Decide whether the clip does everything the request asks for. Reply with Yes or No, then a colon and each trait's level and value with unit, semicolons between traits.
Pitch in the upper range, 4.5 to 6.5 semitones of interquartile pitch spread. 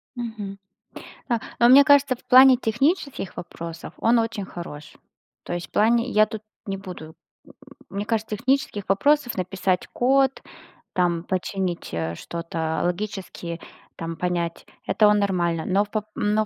Yes: high, 200 Hz; average, 5.1 semitones